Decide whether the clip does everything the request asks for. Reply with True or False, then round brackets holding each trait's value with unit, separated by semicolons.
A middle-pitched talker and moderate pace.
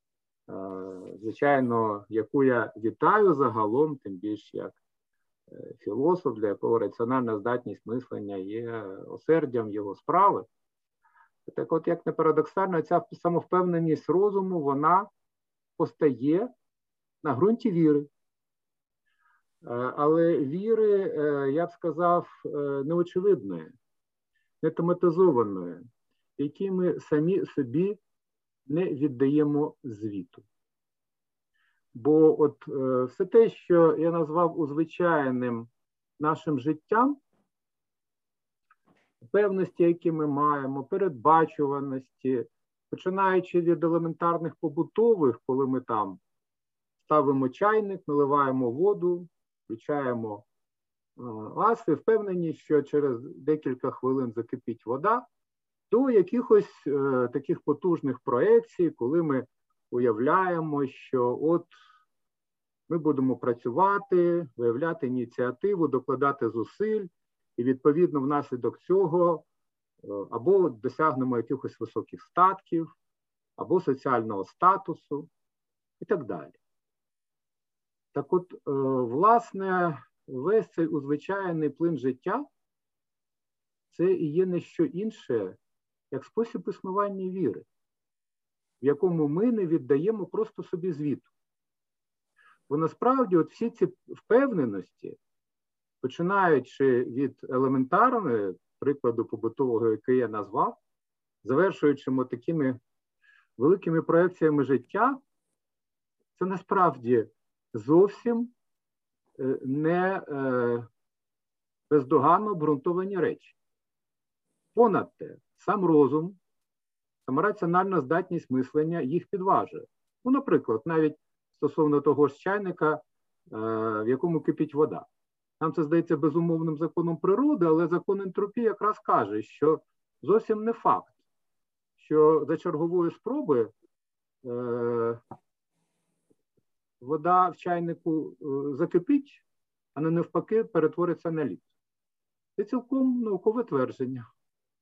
False (160 Hz; 90 wpm)